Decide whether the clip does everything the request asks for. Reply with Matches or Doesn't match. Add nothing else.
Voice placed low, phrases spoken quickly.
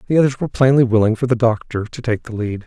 Matches